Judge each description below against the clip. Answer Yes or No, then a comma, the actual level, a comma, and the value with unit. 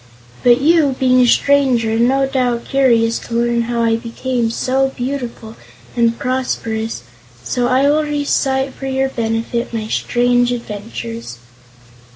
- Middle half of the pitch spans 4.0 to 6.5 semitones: No, narrow, 2.5 semitones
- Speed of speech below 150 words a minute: Yes, average, 140 wpm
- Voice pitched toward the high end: Yes, high, 245 Hz